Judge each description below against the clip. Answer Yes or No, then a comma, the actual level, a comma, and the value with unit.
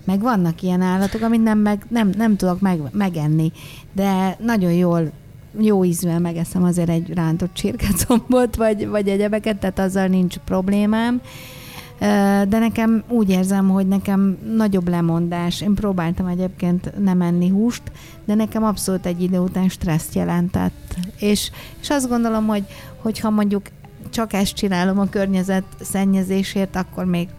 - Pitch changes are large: No, average, 2.9 semitones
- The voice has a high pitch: Yes, high, 195 Hz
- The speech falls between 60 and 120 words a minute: No, average, 145 wpm